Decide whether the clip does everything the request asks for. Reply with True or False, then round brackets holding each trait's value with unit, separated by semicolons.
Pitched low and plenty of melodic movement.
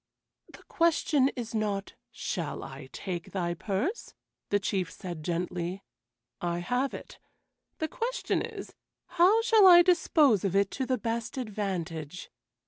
False (205 Hz; 8.5 semitones)